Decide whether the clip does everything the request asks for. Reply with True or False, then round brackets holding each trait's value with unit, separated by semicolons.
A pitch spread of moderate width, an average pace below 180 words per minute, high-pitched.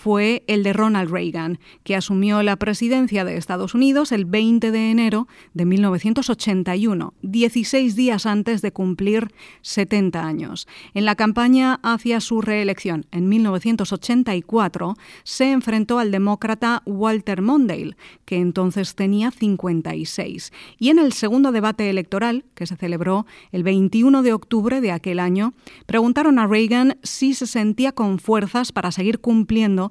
True (3.4 semitones; 140 wpm; 215 Hz)